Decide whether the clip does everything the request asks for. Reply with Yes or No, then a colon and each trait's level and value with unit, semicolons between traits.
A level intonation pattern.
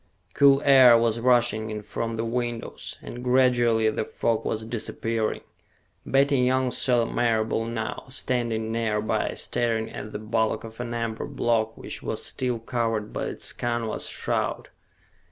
Yes: narrow, 1.6 semitones